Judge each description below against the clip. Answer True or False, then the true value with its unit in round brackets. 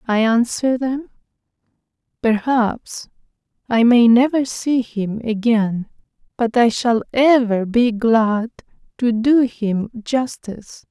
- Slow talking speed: True (110 wpm)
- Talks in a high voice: True (235 Hz)